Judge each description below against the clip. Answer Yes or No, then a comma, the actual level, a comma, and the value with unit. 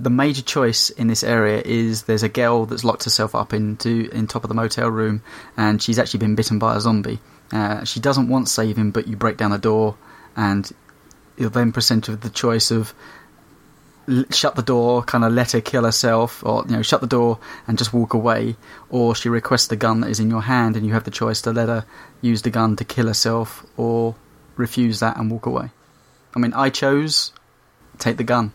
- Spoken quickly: Yes, fast, 225 wpm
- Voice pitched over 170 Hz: No, low, 115 Hz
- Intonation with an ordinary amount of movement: No, narrow, 1.6 semitones